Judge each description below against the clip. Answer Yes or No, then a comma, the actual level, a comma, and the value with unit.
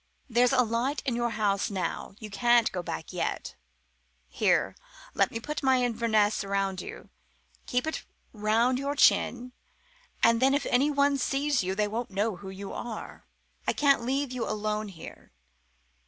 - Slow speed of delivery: No, average, 165 wpm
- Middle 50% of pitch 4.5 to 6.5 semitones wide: No, average, 3.9 semitones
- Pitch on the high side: Yes, high, 230 Hz